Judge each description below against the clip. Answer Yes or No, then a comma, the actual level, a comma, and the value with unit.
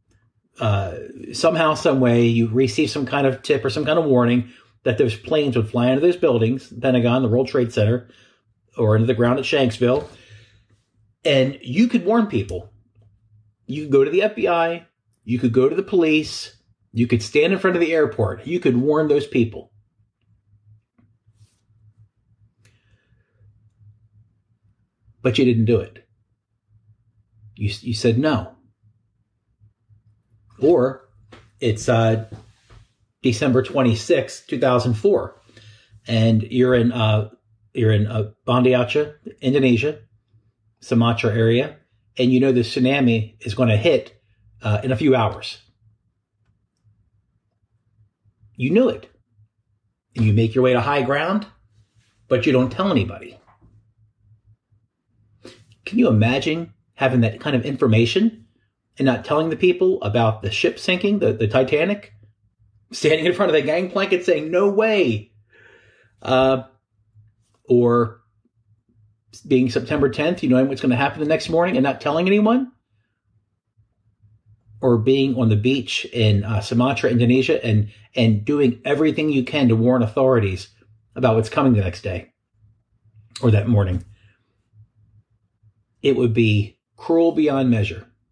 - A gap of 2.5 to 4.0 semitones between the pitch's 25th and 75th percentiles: Yes, average, 3.2 semitones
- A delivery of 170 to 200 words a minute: No, slow, 135 wpm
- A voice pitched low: Yes, low, 115 Hz